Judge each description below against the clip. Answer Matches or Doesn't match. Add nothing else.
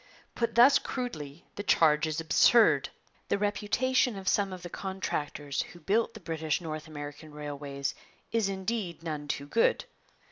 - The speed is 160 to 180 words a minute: Doesn't match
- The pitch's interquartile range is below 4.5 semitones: Doesn't match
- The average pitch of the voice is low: Doesn't match